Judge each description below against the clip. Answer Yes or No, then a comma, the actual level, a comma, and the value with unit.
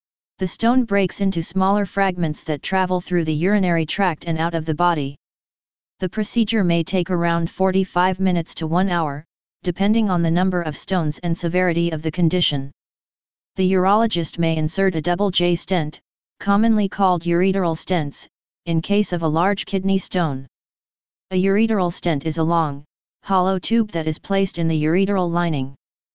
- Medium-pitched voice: Yes, medium, 175 Hz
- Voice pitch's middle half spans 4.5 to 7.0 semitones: No, average, 2.7 semitones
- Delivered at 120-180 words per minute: Yes, average, 165 wpm